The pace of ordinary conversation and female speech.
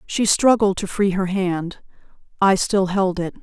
Yes: average, 175 wpm; female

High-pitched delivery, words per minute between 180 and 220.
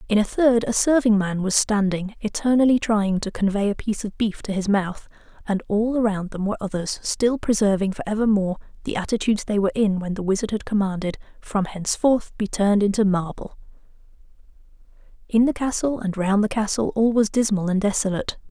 Yes: high, 205 Hz; average, 185 wpm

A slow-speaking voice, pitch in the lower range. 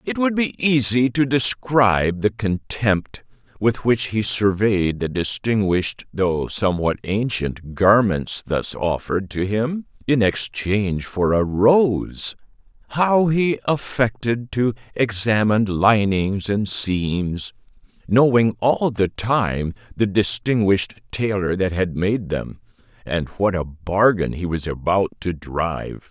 Yes: slow, 120 wpm; low, 105 Hz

